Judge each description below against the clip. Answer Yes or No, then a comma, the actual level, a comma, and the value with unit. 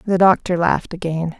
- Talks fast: No, average, 170 wpm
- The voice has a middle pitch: Yes, medium, 180 Hz